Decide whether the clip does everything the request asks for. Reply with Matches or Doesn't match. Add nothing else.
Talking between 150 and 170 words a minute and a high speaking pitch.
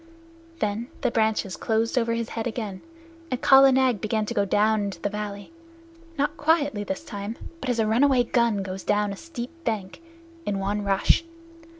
Doesn't match